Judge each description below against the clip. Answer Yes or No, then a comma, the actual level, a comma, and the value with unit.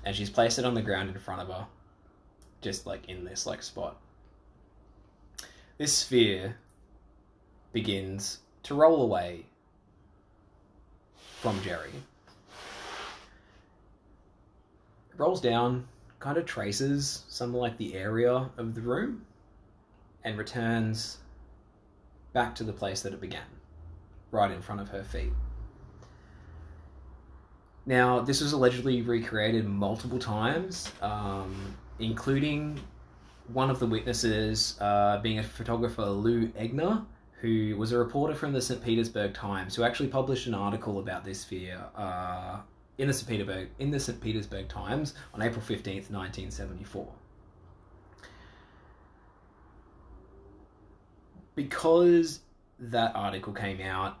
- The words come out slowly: Yes, slow, 120 wpm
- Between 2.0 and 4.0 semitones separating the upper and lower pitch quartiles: Yes, average, 3.6 semitones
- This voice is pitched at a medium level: No, low, 105 Hz